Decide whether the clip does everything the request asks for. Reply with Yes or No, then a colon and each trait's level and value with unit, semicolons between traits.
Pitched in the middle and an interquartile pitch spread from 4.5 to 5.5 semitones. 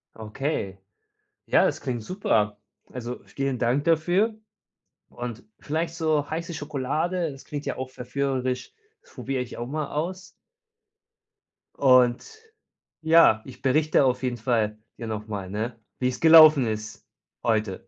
No: low, 130 Hz; average, 4.9 semitones